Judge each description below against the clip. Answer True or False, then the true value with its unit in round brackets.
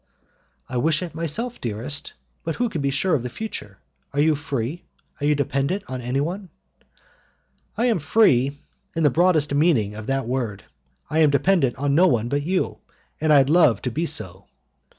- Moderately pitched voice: True (145 Hz)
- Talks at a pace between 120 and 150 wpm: False (180 wpm)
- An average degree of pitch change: True (4.6 semitones)